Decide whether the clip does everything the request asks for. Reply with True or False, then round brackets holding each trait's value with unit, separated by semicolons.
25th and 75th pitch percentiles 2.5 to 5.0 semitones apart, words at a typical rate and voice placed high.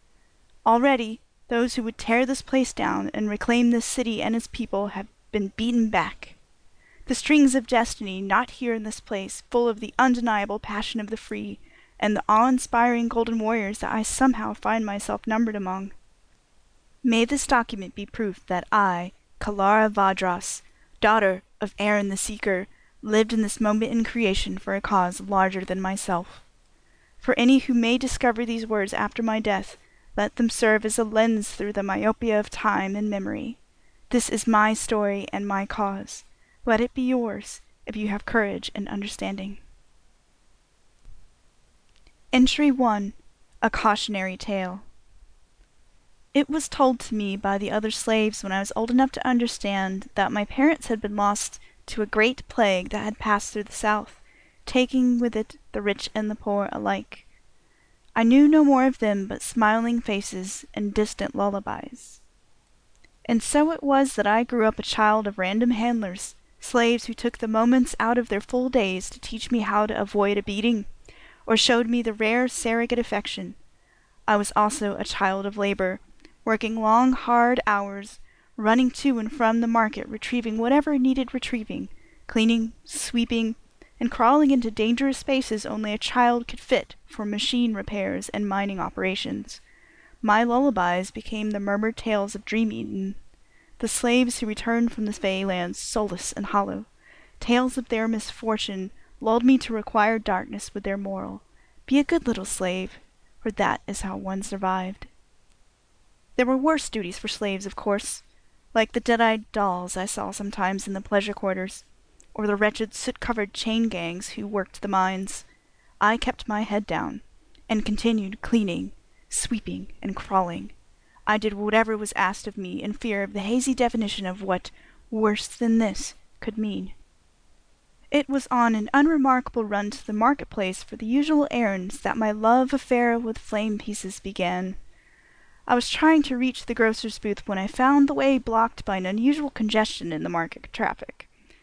True (2.9 semitones; 170 wpm; 220 Hz)